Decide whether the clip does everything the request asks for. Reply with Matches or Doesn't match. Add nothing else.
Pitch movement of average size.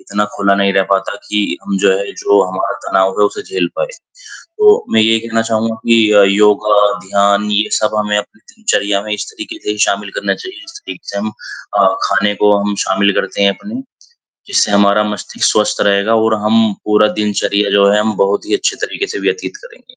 Doesn't match